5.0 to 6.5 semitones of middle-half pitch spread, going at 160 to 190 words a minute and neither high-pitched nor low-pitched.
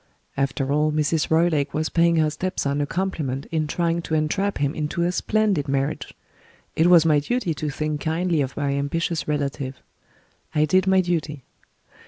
No: average, 2.9 semitones; average, 175 wpm; medium, 155 Hz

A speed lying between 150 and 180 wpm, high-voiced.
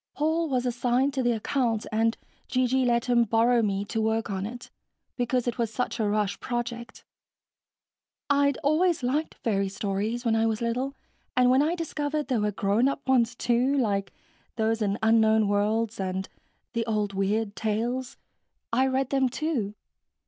Yes: average, 165 wpm; high, 235 Hz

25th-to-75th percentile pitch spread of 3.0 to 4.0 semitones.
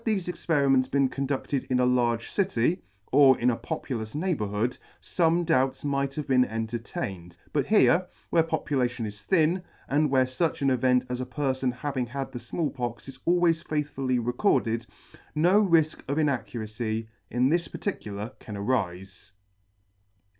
No: average, 4.5 semitones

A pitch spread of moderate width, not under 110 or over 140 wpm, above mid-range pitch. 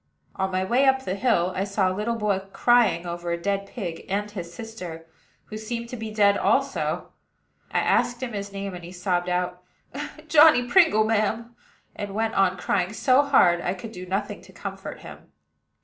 No: average, 4.2 semitones; average, 185 wpm; high, 200 Hz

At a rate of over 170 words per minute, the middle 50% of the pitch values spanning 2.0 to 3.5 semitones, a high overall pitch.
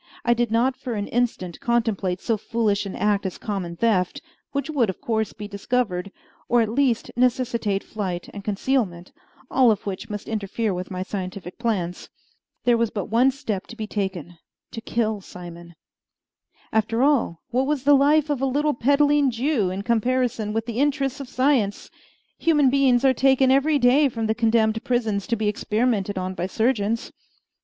No: average, 180 wpm; average, 4.3 semitones; high, 225 Hz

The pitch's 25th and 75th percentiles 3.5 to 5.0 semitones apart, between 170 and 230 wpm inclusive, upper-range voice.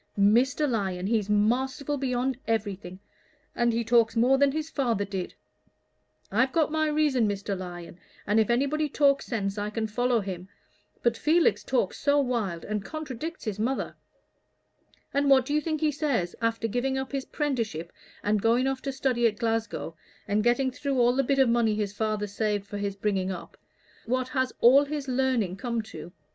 Yes: average, 4.6 semitones; average, 180 wpm; high, 235 Hz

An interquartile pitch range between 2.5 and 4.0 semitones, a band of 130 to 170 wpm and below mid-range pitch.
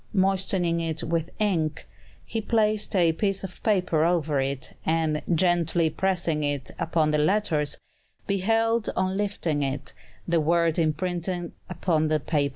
No: average, 3.6 semitones; average, 140 wpm; medium, 170 Hz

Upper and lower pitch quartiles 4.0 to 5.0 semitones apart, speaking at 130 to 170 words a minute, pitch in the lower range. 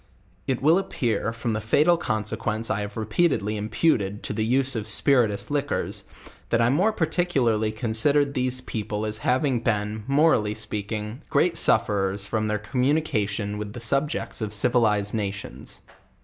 Yes: average, 4.4 semitones; average, 160 wpm; low, 110 Hz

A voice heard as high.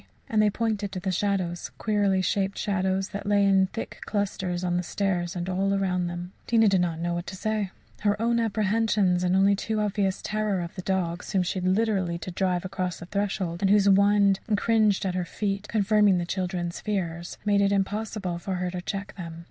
Yes: high, 195 Hz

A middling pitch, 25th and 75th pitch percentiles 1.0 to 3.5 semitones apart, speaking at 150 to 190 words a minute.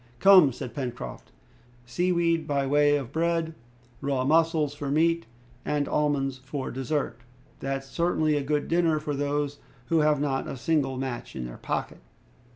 Yes: medium, 145 Hz; average, 2.9 semitones; average, 160 wpm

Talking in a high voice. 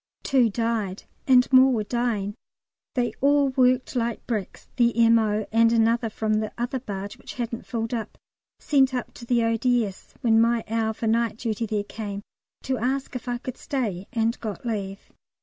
Yes: high, 230 Hz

